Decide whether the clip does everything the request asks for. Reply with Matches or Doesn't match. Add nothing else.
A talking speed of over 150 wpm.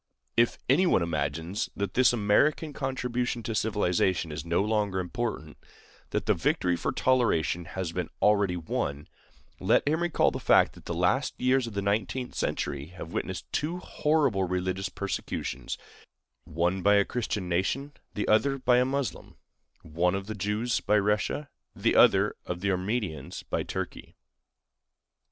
Doesn't match